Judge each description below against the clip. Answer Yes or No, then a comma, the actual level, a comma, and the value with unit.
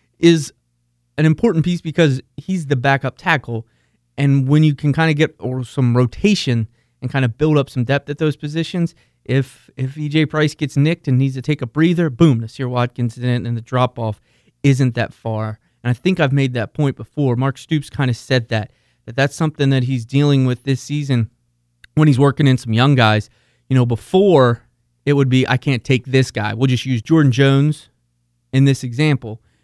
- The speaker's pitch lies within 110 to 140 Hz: Yes, low, 135 Hz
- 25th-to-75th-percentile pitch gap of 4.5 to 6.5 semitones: No, average, 3.4 semitones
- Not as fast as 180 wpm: No, fast, 205 wpm